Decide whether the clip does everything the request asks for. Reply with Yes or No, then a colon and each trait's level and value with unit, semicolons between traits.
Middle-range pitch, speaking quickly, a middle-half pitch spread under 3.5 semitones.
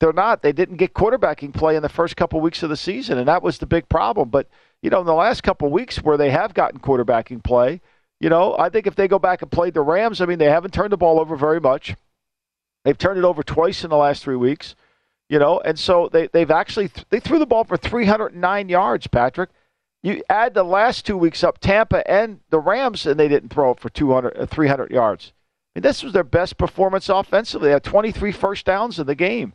No: medium, 175 Hz; fast, 240 wpm; average, 4.7 semitones